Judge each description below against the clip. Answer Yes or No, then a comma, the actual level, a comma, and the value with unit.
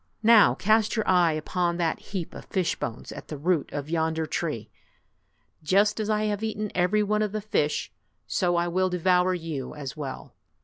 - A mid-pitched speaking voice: Yes, medium, 180 Hz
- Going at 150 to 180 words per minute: No, average, 190 wpm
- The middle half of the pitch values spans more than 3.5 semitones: Yes, average, 4.6 semitones